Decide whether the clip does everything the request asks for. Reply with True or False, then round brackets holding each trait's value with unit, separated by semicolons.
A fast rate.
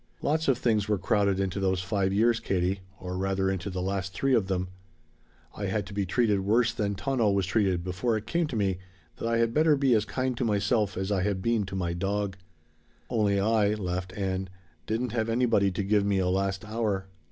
True (215 wpm)